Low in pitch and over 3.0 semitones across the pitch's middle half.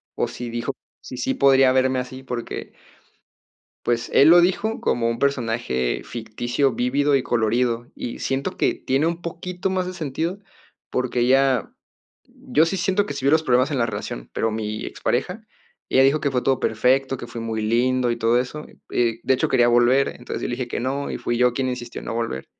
No: low, 125 Hz; average, 2.7 semitones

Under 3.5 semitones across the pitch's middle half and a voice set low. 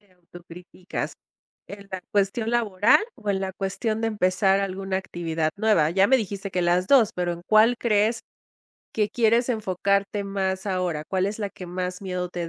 No: narrow, 2.6 semitones; high, 195 Hz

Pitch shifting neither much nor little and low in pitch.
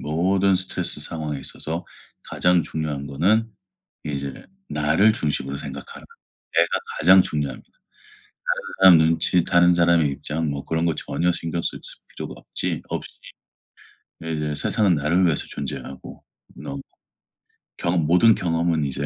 Yes: average, 3.0 semitones; very low, 80 Hz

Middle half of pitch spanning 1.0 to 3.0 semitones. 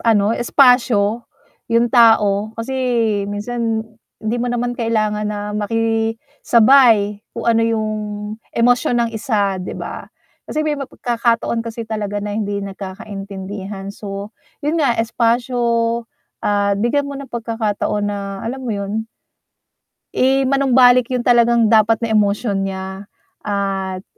Yes: average, 2.7 semitones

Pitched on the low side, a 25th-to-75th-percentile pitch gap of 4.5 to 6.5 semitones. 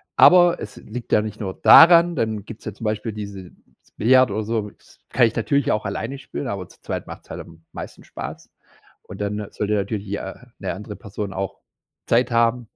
No: low, 105 Hz; narrow, 2.6 semitones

